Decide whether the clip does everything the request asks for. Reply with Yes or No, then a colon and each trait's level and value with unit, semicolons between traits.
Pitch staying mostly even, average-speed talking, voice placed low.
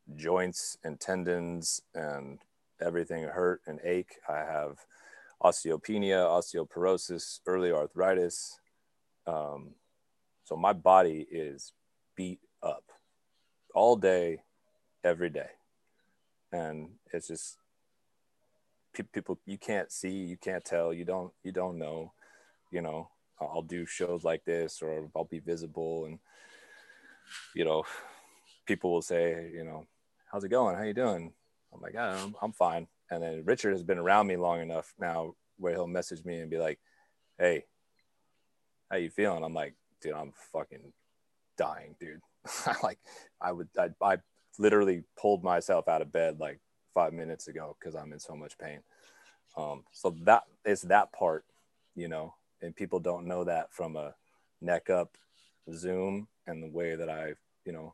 Yes: narrow, 2.3 semitones; average, 150 wpm; very low, 85 Hz